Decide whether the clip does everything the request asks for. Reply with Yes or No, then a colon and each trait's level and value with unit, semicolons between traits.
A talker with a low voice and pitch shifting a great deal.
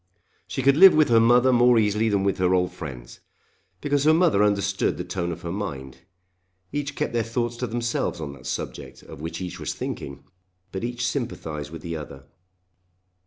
Yes: low, 105 Hz; wide, 6.4 semitones